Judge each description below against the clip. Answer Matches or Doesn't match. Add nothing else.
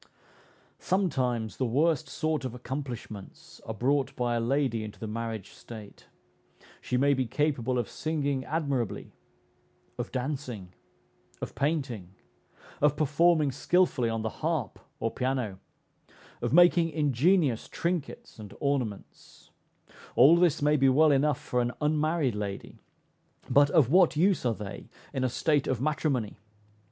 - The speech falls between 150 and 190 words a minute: Doesn't match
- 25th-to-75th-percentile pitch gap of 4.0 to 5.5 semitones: Matches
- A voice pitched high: Doesn't match